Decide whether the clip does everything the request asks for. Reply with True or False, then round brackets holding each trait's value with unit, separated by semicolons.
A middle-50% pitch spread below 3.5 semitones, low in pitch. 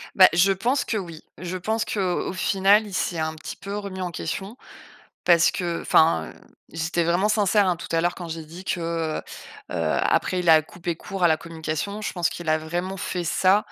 False (2.8 semitones; 175 Hz)